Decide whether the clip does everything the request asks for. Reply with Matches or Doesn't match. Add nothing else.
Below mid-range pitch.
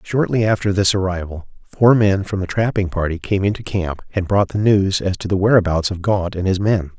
Matches